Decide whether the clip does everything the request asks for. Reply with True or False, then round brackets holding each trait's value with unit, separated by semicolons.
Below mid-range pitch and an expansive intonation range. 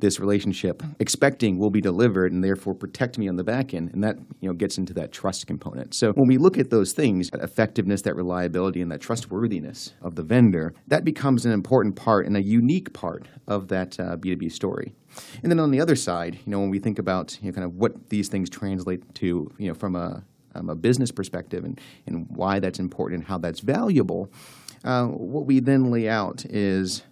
False (100 Hz; 4.4 semitones)